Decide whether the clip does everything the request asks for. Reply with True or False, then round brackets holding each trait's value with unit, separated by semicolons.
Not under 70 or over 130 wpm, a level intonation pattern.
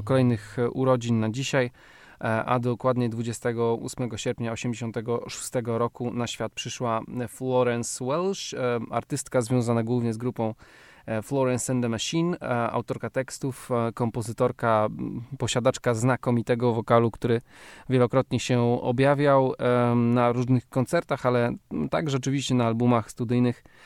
True (110 wpm; 1.6 semitones)